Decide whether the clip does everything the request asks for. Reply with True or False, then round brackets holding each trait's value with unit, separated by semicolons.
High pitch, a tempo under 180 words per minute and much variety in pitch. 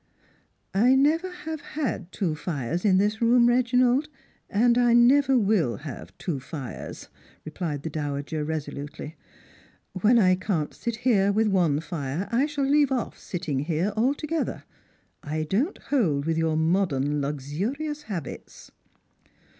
True (195 Hz; 140 wpm; 8.2 semitones)